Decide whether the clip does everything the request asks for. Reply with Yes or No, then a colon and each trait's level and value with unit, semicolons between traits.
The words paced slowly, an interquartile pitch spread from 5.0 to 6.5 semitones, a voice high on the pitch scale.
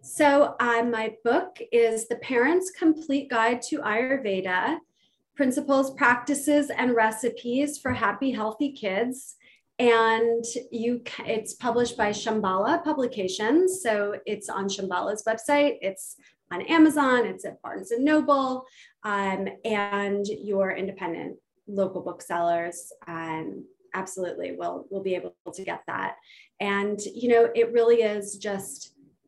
Yes: slow, 125 wpm; average, 5.3 semitones; high, 230 Hz